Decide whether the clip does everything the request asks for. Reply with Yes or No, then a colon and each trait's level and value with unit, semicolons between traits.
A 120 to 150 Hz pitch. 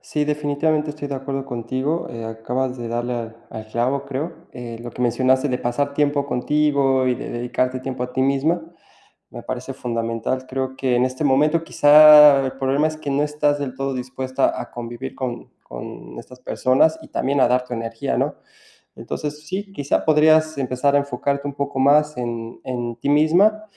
Yes: low, 135 Hz